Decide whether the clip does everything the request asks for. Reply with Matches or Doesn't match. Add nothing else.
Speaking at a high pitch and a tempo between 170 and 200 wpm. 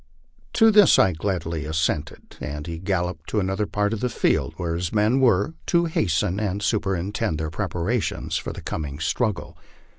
Doesn't match